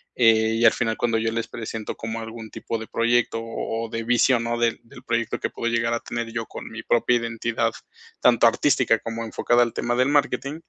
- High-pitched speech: No, low, 115 Hz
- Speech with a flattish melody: Yes, narrow, 1.0 semitones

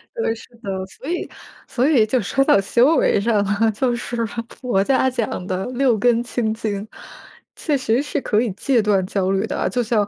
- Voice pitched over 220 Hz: Yes, high, 230 Hz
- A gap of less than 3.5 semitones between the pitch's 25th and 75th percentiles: No, average, 3.8 semitones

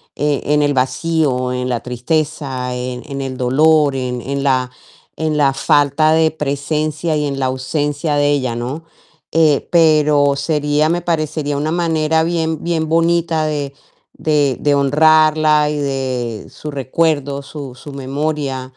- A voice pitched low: No, medium, 145 Hz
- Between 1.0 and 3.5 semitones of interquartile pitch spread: Yes, narrow, 2.6 semitones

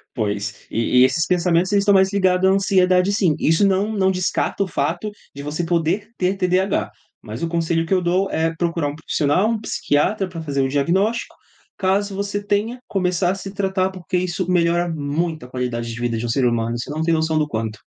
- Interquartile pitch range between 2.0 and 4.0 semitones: No, average, 4.7 semitones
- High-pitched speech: No, medium, 175 Hz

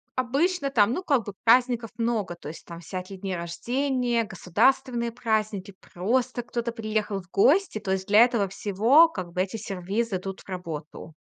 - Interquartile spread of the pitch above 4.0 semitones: Yes, average, 4.4 semitones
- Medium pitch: No, high, 215 Hz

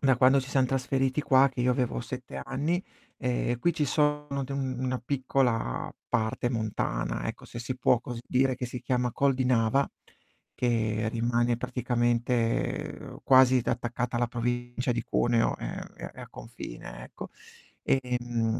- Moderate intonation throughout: No, narrow, 1.8 semitones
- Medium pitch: No, low, 125 Hz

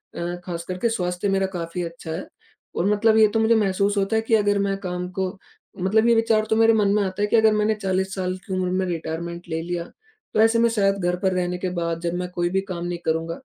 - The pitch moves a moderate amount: Yes, average, 3.3 semitones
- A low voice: No, high, 190 Hz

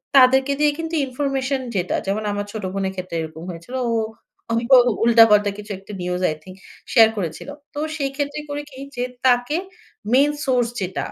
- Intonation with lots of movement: Yes, wide, 5.9 semitones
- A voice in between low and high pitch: No, high, 235 Hz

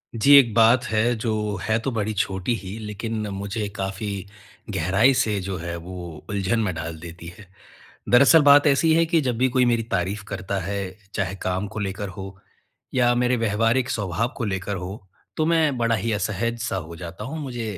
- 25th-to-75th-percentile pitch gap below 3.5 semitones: No, average, 4.1 semitones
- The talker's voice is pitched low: Yes, low, 110 Hz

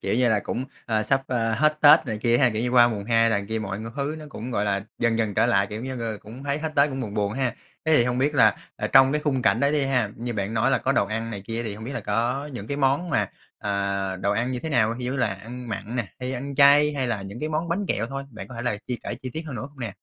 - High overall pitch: No, low, 120 Hz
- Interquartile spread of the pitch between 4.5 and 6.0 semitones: No, average, 4.0 semitones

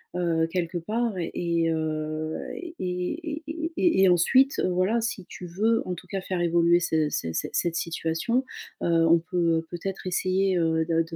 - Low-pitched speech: No, medium, 175 Hz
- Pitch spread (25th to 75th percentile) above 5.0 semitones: No, average, 2.9 semitones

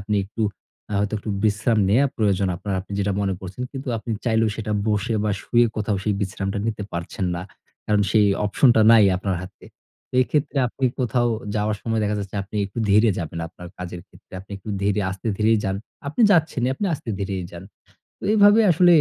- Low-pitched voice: Yes, low, 105 Hz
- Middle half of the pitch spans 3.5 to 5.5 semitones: No, average, 3.0 semitones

